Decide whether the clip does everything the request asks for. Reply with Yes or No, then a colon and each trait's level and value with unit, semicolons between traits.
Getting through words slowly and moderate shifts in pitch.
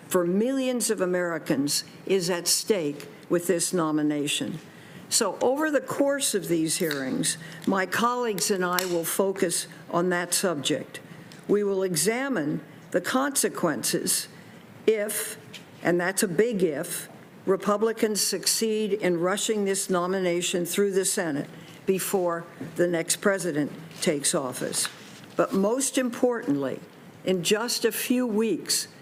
Yes: slow, 125 wpm; average, 4.0 semitones